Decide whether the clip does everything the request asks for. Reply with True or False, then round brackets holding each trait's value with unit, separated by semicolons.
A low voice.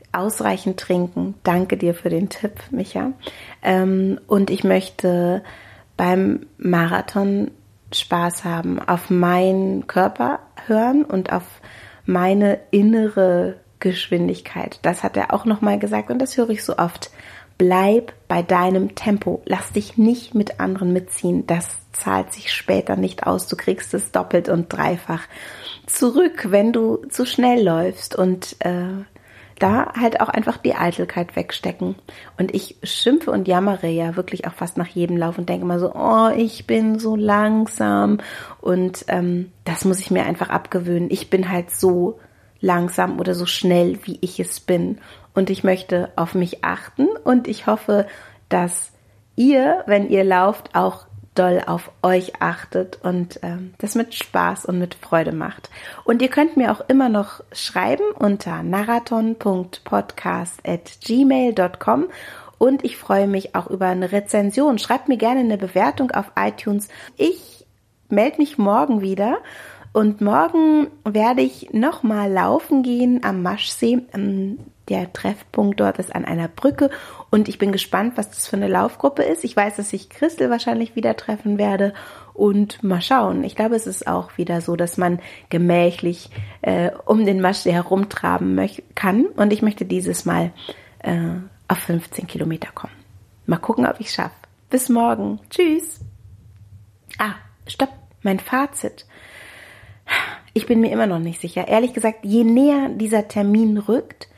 False (190 Hz)